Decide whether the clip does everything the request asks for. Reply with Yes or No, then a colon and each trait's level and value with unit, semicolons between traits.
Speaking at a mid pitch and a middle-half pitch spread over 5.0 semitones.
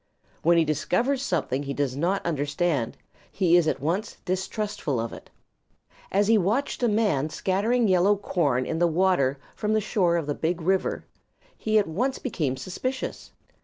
Yes: medium, 175 Hz; wide, 5.6 semitones